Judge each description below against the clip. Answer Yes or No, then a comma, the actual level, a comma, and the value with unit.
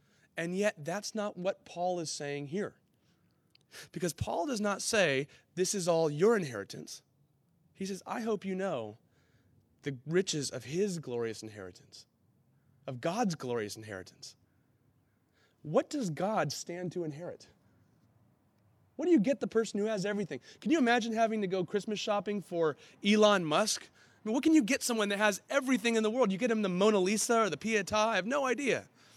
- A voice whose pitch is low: No, high, 190 Hz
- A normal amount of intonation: No, wide, 7.0 semitones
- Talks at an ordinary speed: Yes, average, 180 wpm